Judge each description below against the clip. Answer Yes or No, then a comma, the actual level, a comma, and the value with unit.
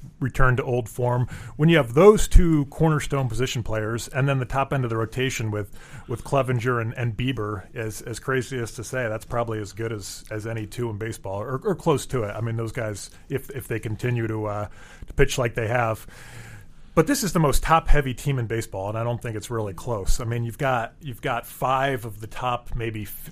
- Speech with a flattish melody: No, average, 3.1 semitones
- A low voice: Yes, low, 120 Hz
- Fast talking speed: Yes, fast, 235 wpm